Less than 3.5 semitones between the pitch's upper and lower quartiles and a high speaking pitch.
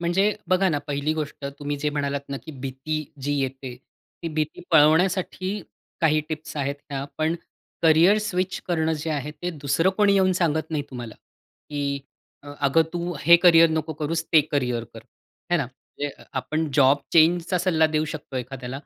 No: average, 3.1 semitones; medium, 155 Hz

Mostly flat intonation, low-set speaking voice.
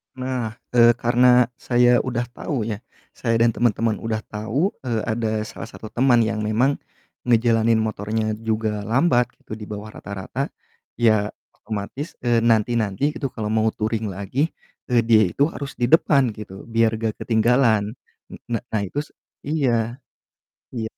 Yes: narrow, 2.1 semitones; low, 115 Hz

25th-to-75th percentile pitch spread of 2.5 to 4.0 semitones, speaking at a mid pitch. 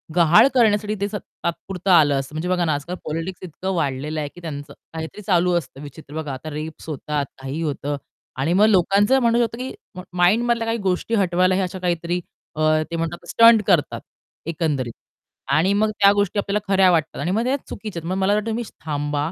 No: average, 4.6 semitones; medium, 175 Hz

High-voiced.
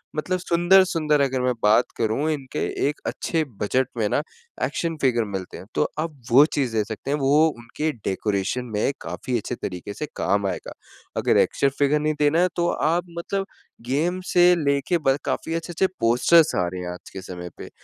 No: medium, 140 Hz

